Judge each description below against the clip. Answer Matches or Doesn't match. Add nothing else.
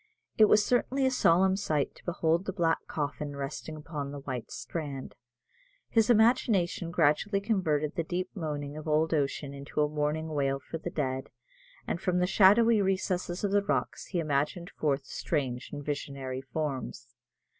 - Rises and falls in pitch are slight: Doesn't match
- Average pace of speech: Matches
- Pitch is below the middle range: Doesn't match